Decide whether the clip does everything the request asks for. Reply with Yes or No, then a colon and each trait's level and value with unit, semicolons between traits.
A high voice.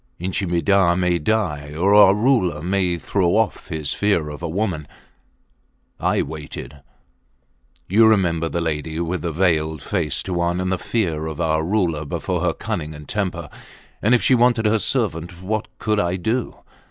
No: very low, 90 Hz